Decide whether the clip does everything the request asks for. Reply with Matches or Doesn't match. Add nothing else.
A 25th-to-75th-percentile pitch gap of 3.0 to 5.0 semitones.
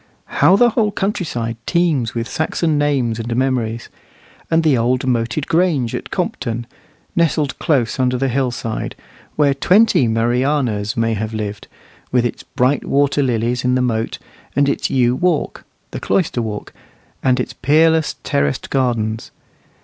Matches